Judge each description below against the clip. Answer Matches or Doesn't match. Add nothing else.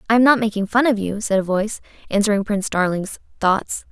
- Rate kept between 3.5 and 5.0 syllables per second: Doesn't match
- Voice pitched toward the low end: Doesn't match